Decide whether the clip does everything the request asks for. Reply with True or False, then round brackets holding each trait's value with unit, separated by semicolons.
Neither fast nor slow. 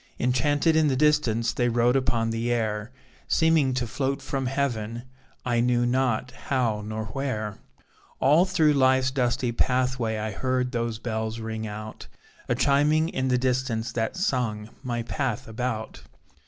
True (150 wpm)